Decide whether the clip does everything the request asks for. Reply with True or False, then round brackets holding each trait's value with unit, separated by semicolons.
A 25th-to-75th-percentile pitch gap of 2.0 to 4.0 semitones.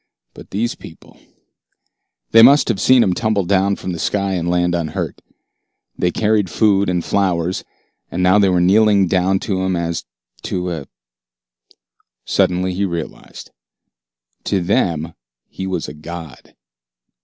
True (2.4 semitones)